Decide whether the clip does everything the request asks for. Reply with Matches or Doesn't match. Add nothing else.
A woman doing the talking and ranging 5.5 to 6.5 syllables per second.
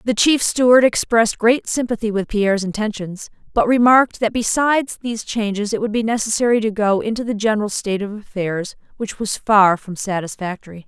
Matches